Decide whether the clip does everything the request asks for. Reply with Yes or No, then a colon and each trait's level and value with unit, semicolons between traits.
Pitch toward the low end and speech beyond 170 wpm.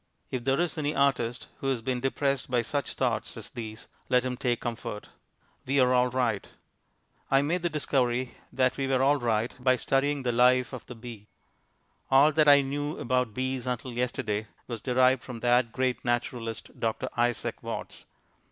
Yes: low, 125 Hz; average, 180 wpm